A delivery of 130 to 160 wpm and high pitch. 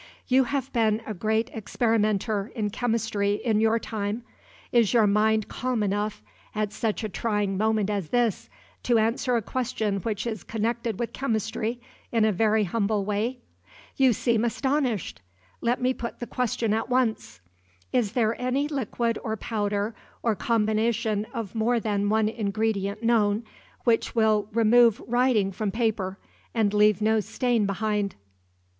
Yes: average, 150 wpm; high, 220 Hz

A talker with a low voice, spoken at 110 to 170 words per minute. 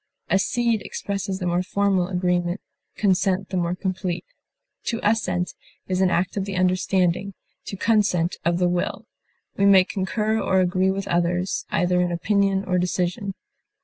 No: medium, 185 Hz; average, 150 wpm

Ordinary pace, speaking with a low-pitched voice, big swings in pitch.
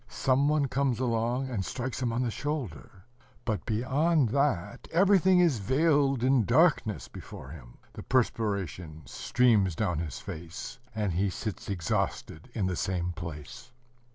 Yes: average, 145 wpm; low, 115 Hz; wide, 6.8 semitones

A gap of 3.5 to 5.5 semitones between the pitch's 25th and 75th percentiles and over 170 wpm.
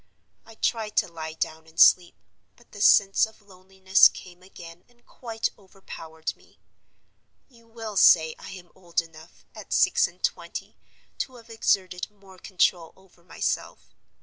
No: average, 4.3 semitones; average, 150 wpm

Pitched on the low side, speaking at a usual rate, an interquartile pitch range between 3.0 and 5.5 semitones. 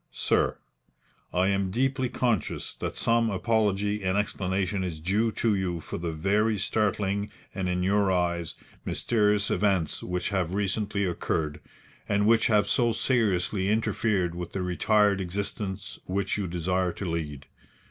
No: low, 100 Hz; average, 145 wpm; narrow, 2.6 semitones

